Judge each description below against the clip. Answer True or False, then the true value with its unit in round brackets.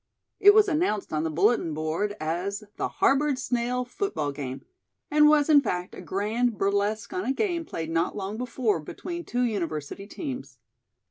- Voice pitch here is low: False (215 Hz)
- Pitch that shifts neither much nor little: False (7.6 semitones)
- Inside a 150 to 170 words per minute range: True (165 wpm)